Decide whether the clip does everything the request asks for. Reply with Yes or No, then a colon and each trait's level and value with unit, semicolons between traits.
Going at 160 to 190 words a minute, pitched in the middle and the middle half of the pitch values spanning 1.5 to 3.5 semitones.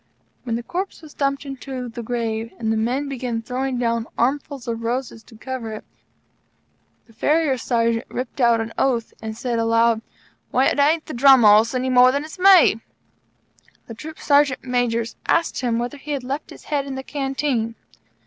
No: average, 185 wpm; very high, 250 Hz; average, 3.2 semitones